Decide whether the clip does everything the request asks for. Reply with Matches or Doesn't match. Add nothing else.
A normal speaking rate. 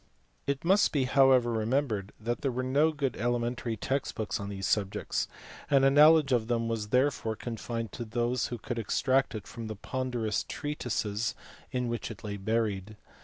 Matches